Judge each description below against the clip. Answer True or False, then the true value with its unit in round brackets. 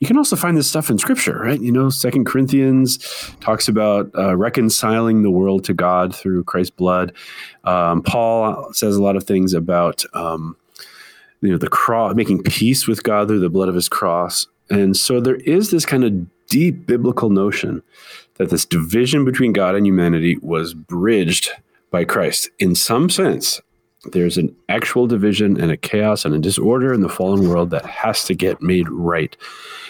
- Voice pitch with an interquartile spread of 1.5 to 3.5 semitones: False (5.4 semitones)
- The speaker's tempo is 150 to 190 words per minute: True (185 wpm)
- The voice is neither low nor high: False (100 Hz)